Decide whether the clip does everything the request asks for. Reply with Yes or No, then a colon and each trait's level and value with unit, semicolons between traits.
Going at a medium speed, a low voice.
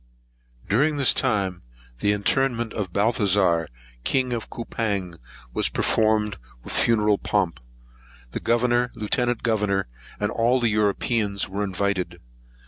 No: slow, 125 wpm; low, 105 Hz